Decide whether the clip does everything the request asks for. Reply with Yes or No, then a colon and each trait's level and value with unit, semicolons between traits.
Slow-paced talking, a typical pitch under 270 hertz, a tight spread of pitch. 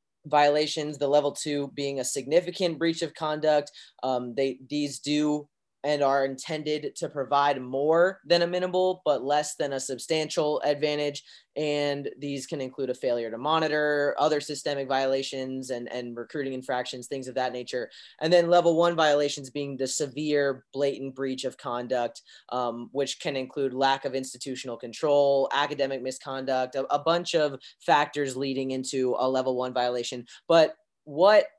No: average, 160 wpm; medium, 140 Hz; narrow, 2.3 semitones